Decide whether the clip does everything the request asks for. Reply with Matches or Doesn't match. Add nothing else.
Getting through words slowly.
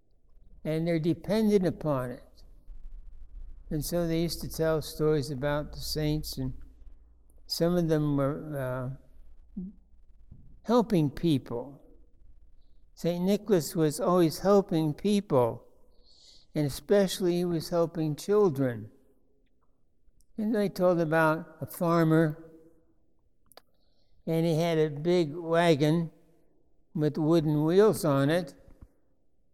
Matches